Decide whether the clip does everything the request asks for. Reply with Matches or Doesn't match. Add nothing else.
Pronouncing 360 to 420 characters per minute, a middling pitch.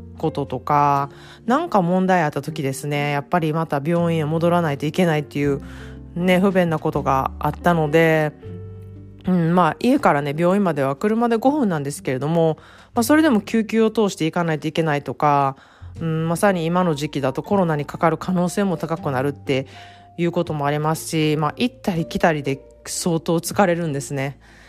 Matches